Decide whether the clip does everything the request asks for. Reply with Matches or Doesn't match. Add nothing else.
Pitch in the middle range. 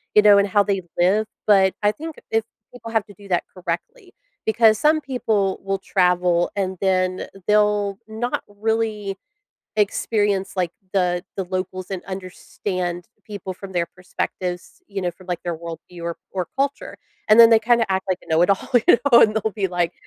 Doesn't match